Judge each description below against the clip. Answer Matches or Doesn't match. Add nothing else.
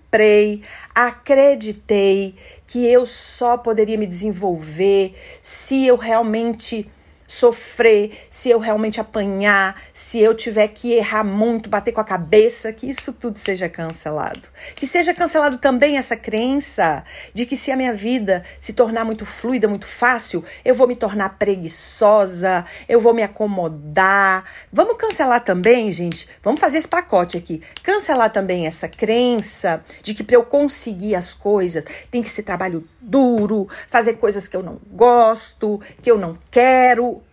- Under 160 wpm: Matches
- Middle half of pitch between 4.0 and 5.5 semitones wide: Doesn't match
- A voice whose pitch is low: Doesn't match